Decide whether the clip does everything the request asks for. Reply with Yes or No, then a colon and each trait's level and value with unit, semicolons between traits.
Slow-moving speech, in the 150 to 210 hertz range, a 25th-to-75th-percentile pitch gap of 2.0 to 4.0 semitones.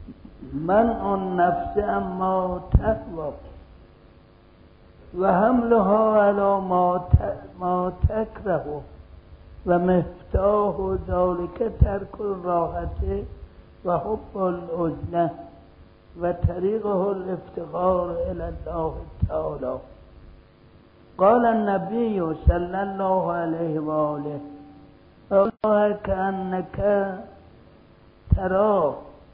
Yes: slow, 60 wpm; medium, 185 Hz; average, 3.0 semitones